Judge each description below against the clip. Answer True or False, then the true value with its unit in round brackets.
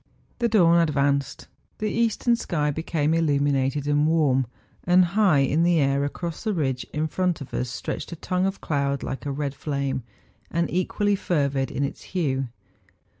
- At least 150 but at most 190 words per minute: True (170 wpm)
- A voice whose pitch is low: False (150 Hz)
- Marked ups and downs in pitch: False (4.0 semitones)